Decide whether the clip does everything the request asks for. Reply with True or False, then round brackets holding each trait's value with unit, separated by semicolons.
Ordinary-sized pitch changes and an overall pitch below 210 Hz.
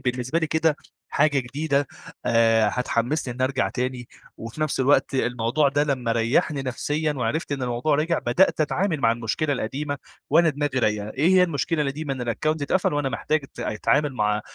True (3.9 semitones; 140 Hz)